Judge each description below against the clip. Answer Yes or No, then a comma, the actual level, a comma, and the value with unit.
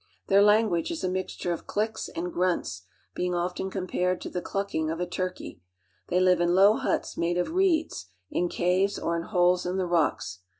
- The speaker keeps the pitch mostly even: Yes, narrow, 1.9 semitones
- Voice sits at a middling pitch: Yes, medium, 180 Hz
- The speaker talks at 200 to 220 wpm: Yes, fast, 205 wpm